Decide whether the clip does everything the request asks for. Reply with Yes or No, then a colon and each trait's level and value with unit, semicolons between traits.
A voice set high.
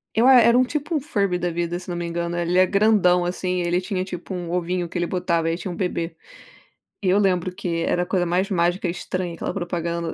No: medium, 180 Hz